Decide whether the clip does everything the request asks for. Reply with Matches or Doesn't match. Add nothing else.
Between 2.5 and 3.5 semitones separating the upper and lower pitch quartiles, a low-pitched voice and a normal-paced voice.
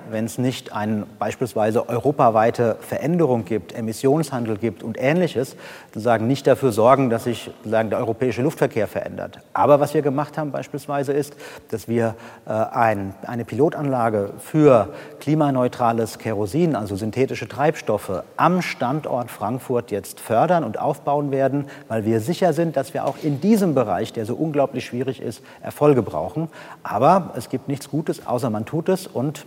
Doesn't match